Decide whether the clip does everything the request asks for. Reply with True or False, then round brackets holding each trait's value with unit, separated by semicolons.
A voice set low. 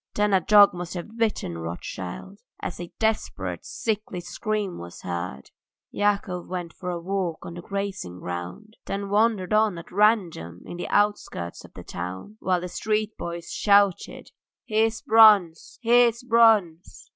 False (195 Hz)